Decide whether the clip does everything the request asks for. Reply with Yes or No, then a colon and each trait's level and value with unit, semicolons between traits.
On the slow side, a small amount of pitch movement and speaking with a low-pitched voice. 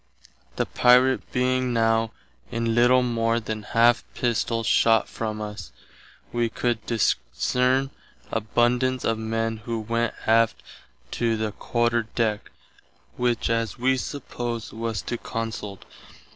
Yes: slow, 120 wpm; narrow, 1.3 semitones; low, 115 Hz